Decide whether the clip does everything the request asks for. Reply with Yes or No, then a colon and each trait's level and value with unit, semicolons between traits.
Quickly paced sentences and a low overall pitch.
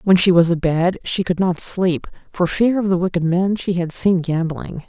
No: fast, 220 wpm; medium, 175 Hz